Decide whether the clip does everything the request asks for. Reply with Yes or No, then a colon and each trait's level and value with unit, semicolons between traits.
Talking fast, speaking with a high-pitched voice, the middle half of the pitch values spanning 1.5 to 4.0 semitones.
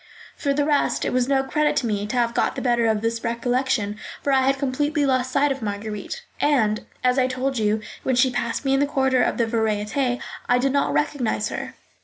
Yes: fast, 225 wpm; very high, 255 Hz; average, 3.3 semitones